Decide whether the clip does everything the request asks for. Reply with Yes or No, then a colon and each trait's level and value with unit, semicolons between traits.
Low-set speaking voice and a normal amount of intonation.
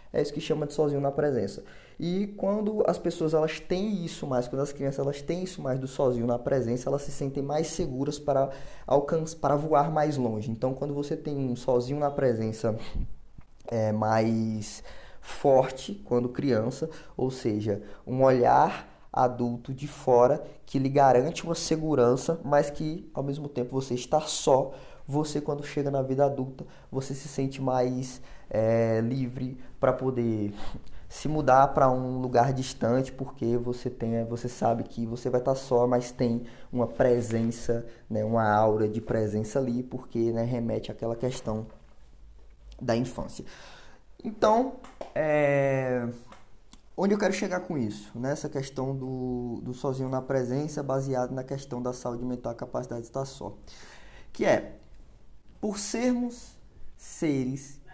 Yes: low, 130 Hz; average, 3.3 semitones